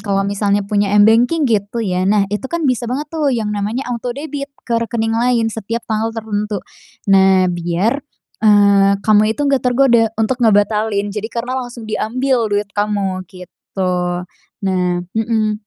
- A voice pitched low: No, high, 220 Hz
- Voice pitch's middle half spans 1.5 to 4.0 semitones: Yes, average, 2.9 semitones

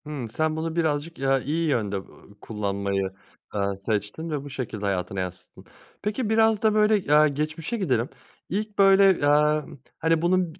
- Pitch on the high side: No, medium, 150 Hz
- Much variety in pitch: Yes, wide, 8.3 semitones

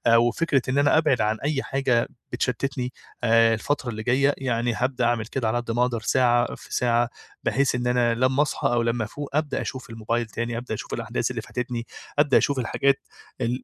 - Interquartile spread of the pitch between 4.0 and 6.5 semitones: No, narrow, 2.4 semitones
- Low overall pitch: Yes, low, 125 Hz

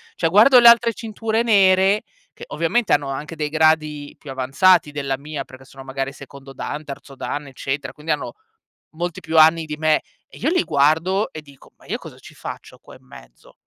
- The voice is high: No, medium, 155 Hz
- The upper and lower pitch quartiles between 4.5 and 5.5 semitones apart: Yes, average, 5.1 semitones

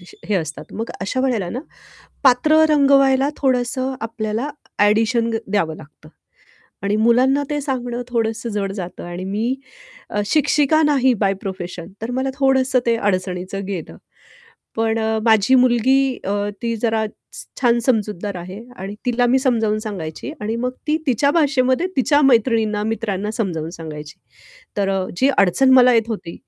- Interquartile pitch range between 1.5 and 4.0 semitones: No, average, 4.5 semitones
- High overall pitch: Yes, high, 225 Hz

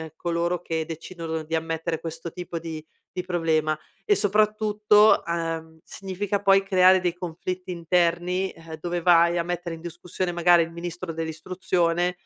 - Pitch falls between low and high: Yes, medium, 175 Hz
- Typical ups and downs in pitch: No, narrow, 1.9 semitones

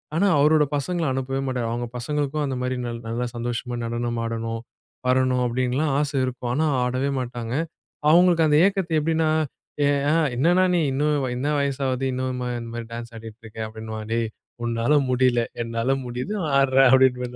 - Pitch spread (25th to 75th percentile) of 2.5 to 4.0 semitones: Yes, average, 3.4 semitones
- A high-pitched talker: No, low, 125 Hz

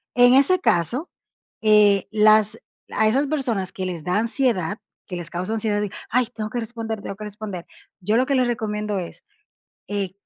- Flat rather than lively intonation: No, average, 3.2 semitones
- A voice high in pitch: Yes, high, 215 Hz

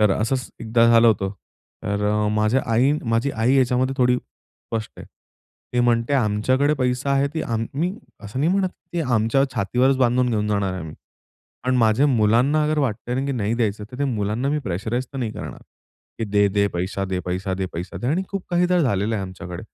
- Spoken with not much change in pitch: No, average, 4.2 semitones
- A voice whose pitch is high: No, low, 115 Hz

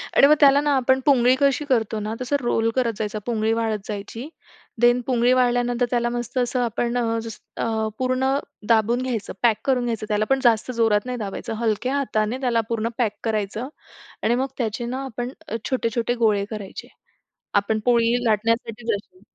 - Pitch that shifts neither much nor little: No, narrow, 2.3 semitones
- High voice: Yes, high, 235 Hz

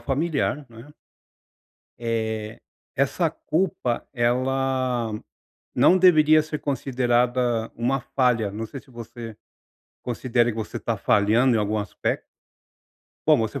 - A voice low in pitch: Yes, low, 120 Hz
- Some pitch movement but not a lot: Yes, average, 3.0 semitones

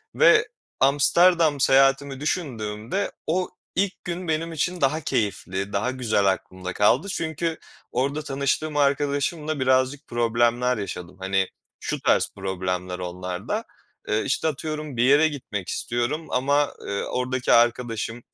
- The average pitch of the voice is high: No, low, 130 Hz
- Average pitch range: No, wide, 6.1 semitones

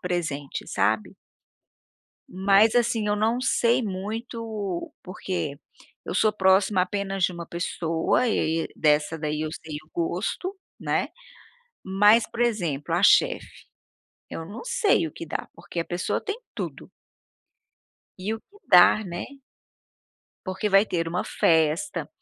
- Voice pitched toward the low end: No, high, 190 Hz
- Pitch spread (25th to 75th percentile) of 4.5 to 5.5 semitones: Yes, average, 4.8 semitones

